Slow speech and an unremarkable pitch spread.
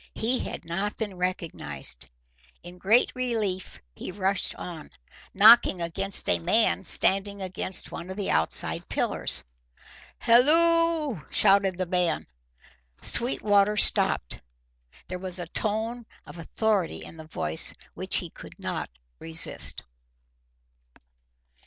Yes: slow, 115 wpm; average, 3.9 semitones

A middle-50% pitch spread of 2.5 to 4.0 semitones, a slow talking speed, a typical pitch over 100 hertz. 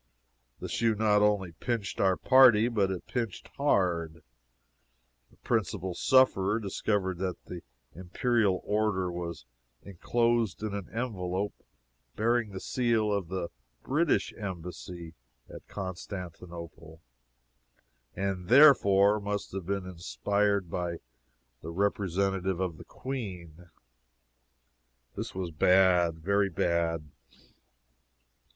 No: average, 3.3 semitones; slow, 105 wpm; very low, 95 Hz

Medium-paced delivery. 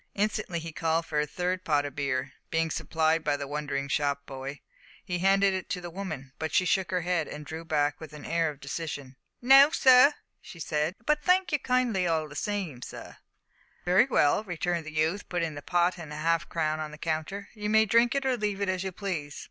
No: fast, 220 wpm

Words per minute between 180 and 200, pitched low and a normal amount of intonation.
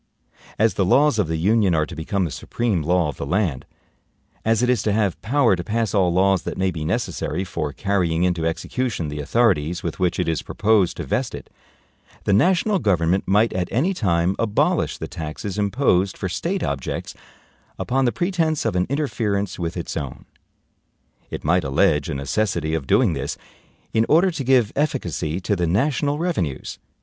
No: average, 185 wpm; very low, 95 Hz; wide, 5.8 semitones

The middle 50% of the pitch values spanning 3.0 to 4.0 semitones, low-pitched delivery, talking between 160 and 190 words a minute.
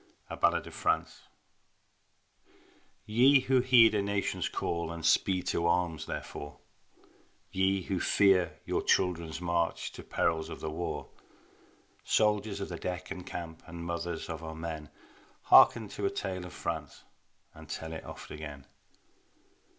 No: average, 3.3 semitones; very low, 90 Hz; average, 145 wpm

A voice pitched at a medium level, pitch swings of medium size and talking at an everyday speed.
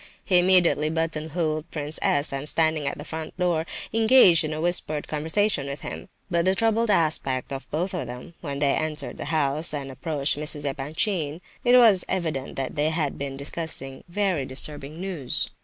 Yes: medium, 155 Hz; average, 3.6 semitones; average, 180 wpm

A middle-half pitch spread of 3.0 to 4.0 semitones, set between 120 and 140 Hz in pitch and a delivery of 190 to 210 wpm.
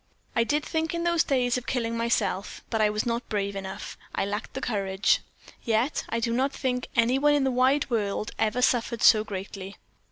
No: average, 3.7 semitones; high, 230 Hz; average, 200 wpm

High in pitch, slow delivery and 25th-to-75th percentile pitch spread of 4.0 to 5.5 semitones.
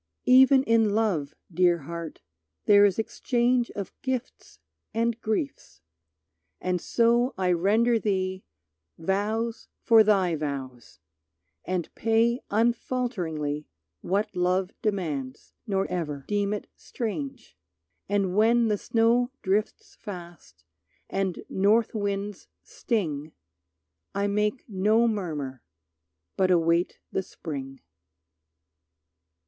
Yes: high, 200 Hz; slow, 100 wpm; average, 4.8 semitones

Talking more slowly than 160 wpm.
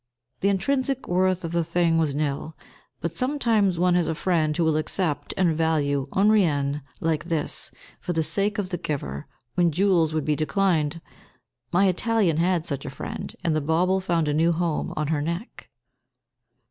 No: average, 180 wpm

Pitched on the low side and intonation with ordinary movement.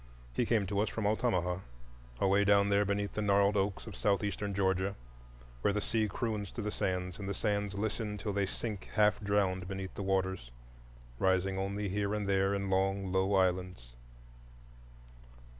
No: low, 100 Hz; narrow, 1.3 semitones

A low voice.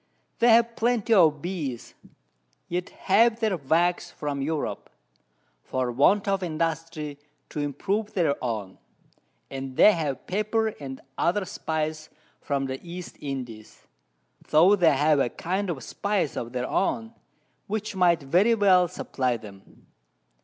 No: medium, 165 Hz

